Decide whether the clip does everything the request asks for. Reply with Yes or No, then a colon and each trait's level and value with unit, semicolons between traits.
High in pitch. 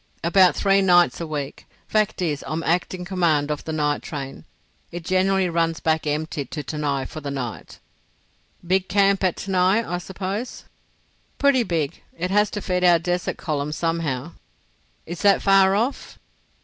No: medium, 175 Hz